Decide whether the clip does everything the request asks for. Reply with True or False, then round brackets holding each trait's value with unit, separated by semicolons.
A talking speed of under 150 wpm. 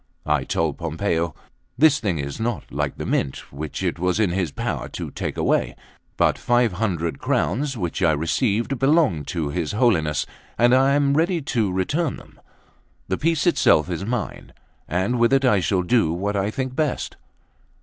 False (175 wpm)